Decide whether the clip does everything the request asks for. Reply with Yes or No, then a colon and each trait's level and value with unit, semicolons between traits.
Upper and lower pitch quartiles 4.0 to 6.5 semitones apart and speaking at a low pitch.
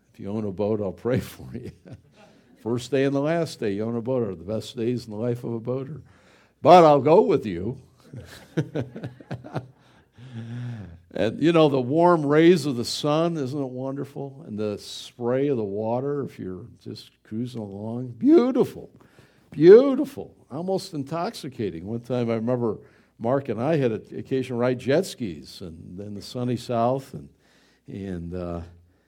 Yes: average, 4.4 semitones; low, 120 Hz